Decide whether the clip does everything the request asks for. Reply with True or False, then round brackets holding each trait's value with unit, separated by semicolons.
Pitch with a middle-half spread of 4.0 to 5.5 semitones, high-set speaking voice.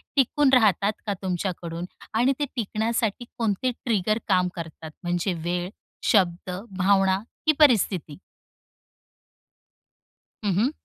True (4.7 semitones; 200 Hz)